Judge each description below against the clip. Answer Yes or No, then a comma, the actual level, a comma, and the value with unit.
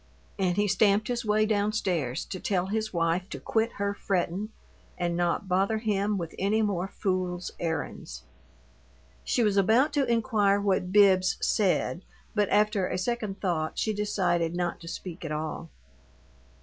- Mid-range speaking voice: No, high, 195 Hz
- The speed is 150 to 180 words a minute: Yes, average, 160 wpm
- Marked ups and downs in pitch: No, average, 3.1 semitones